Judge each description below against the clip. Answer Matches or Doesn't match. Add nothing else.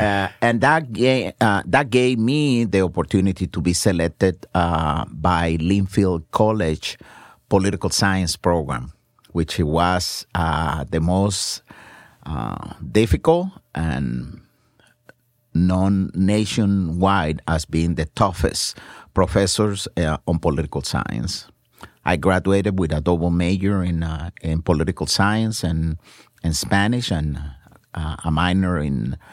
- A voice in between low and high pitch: Doesn't match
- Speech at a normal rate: Doesn't match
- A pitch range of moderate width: Matches